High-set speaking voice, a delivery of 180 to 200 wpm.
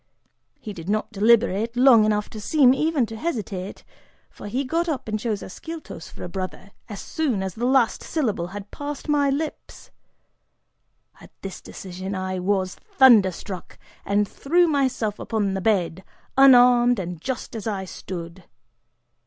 No: high, 215 Hz; average, 155 wpm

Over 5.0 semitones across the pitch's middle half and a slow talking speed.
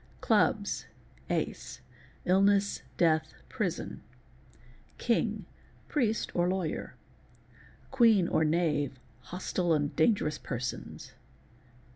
Yes: wide, 5.6 semitones; slow, 60 wpm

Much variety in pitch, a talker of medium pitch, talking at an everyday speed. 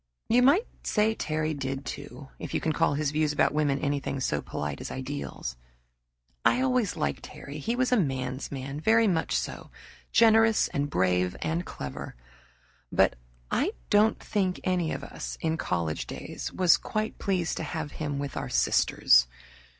Yes: wide, 6.5 semitones; medium, 150 Hz; average, 165 wpm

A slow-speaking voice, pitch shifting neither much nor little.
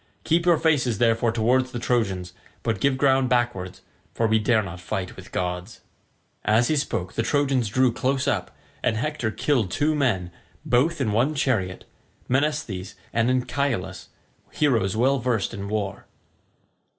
No: average, 150 wpm; average, 4.4 semitones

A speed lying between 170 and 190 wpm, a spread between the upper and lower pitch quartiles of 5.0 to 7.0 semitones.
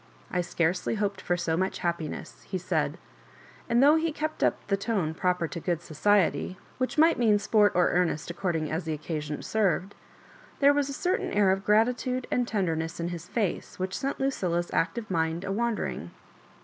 Yes: average, 180 wpm; wide, 5.4 semitones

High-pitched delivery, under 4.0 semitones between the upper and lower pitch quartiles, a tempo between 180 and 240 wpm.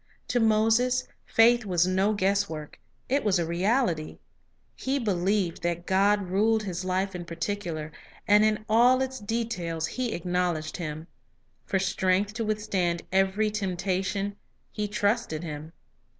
No: high, 195 Hz; average, 3.6 semitones; average, 145 wpm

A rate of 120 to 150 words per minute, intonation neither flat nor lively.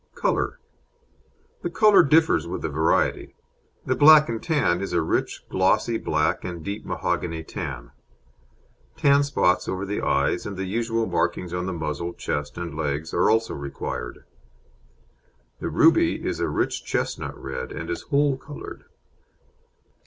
No: average, 145 wpm; wide, 8.9 semitones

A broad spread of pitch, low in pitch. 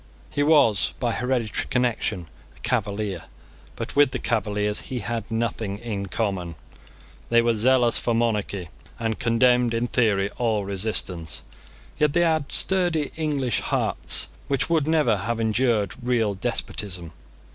No: average, 3.5 semitones; low, 115 Hz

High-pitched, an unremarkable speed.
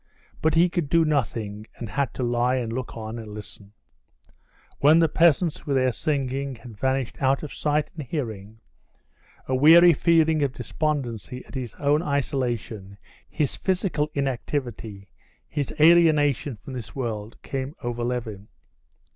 No: low, 130 Hz; average, 145 wpm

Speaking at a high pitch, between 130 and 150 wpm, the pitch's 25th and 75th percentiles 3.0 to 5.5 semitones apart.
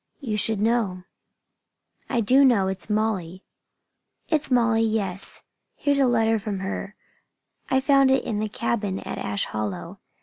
Yes: high, 220 Hz; average, 145 wpm; average, 4.0 semitones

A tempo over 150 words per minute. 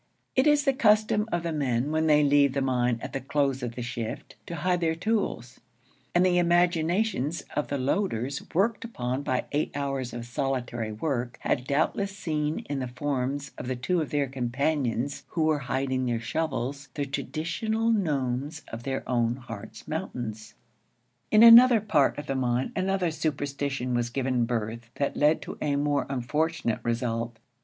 Yes: average, 170 wpm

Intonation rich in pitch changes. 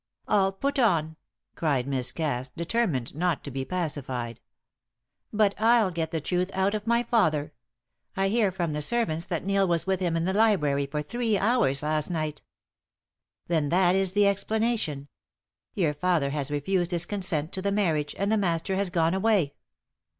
No: average, 4.9 semitones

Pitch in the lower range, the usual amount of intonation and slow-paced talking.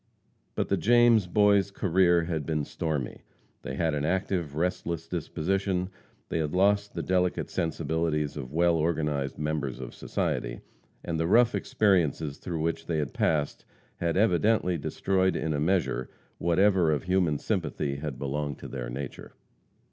No: very low, 80 Hz; average, 3.8 semitones; average, 150 wpm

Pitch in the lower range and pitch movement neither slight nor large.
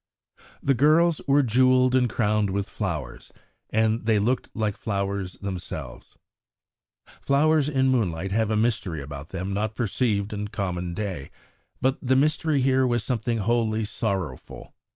Yes: low, 110 Hz; average, 4.5 semitones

